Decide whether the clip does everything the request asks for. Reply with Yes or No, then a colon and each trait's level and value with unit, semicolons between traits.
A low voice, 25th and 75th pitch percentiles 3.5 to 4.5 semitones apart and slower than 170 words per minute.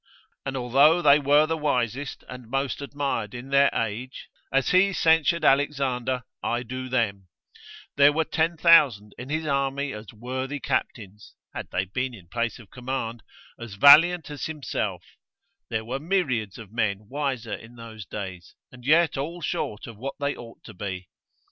Yes: low, 130 Hz; average, 4.1 semitones; average, 160 wpm